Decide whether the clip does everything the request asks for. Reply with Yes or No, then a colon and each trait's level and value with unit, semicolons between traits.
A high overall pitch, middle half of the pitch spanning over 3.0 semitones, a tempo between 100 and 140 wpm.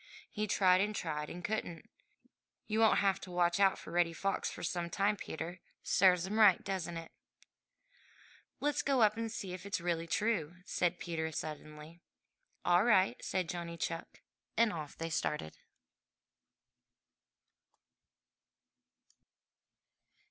No: medium, 180 Hz; average, 3.4 semitones; slow, 135 wpm